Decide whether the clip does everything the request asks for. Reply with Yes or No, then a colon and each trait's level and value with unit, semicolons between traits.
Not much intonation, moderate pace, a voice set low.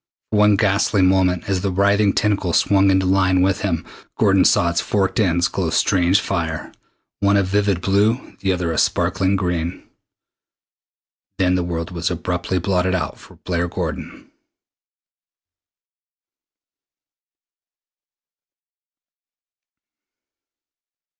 No: narrow, 2.1 semitones; slow, 115 wpm; very low, 95 Hz